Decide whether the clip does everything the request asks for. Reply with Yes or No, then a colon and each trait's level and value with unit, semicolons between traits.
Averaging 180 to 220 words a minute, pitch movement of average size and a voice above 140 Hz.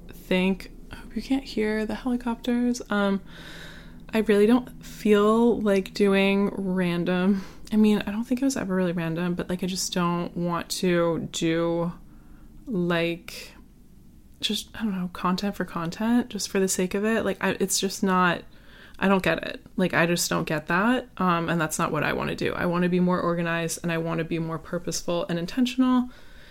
Yes: average, 195 wpm; average, 3.8 semitones; high, 190 Hz